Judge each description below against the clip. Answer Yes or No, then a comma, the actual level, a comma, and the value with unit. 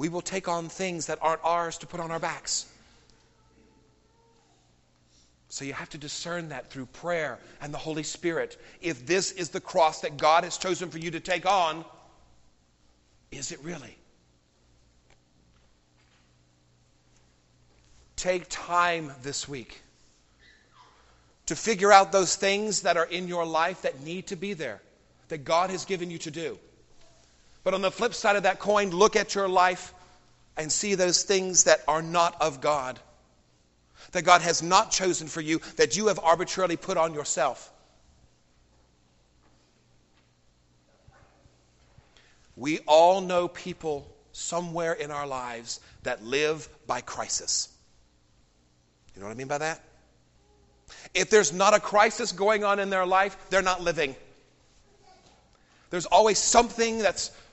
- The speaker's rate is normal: Yes, average, 145 wpm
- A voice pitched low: No, medium, 160 Hz